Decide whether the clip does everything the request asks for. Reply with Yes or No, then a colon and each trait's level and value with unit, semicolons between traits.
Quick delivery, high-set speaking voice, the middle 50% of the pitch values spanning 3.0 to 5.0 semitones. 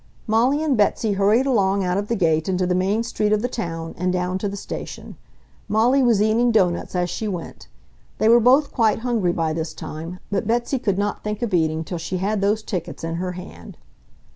Yes: fast, 215 wpm; high, 200 Hz; average, 4.0 semitones